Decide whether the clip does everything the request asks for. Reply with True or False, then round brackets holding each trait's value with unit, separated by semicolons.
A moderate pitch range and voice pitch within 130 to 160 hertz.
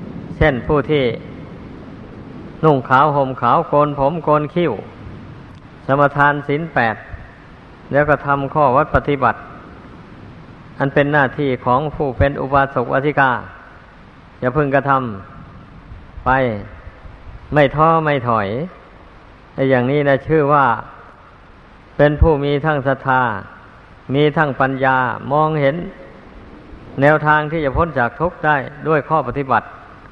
True (3.1 semitones; 140 Hz)